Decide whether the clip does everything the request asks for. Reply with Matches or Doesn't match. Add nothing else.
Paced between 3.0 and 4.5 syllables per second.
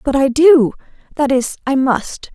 Matches